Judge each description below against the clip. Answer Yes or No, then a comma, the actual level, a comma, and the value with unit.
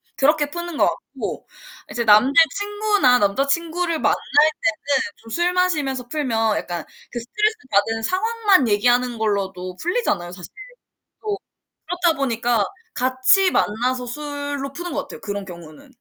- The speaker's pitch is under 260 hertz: No, very high, 270 Hz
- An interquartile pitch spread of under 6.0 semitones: No, wide, 7.6 semitones